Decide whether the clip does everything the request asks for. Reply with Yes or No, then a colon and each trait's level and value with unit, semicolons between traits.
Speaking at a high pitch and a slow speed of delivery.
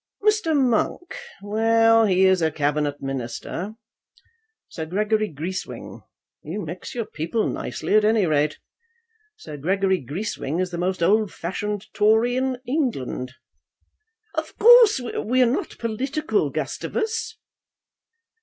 Yes: high, 210 Hz; slow, 120 wpm